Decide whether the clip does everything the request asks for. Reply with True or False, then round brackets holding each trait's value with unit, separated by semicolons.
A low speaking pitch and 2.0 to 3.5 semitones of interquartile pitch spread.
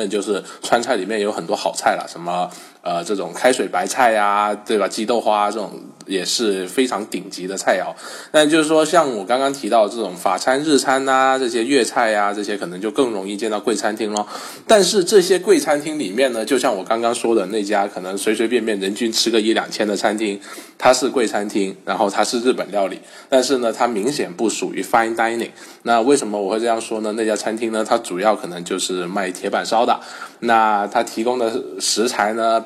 True (115 Hz; 3.1 semitones)